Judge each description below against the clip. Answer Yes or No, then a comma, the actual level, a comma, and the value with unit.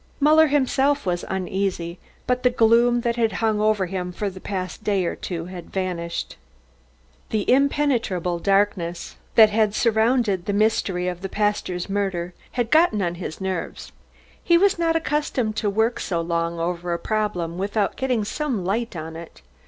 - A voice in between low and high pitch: No, high, 205 Hz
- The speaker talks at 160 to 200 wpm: Yes, average, 165 wpm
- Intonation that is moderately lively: Yes, average, 4.8 semitones